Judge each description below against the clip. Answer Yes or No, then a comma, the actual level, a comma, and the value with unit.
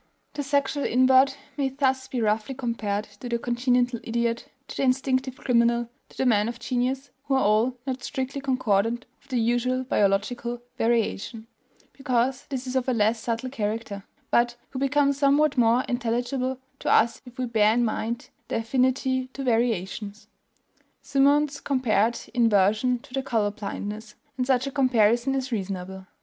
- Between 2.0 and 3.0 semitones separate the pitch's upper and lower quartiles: Yes, average, 2.7 semitones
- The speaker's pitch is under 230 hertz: No, high, 245 Hz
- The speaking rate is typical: Yes, average, 160 wpm